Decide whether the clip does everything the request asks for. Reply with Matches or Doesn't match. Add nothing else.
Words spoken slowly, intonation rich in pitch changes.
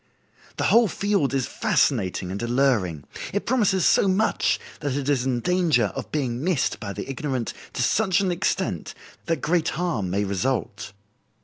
Doesn't match